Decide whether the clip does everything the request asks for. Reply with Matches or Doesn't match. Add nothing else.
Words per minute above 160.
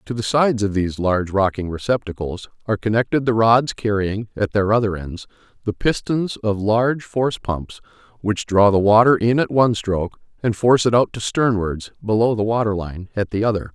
Matches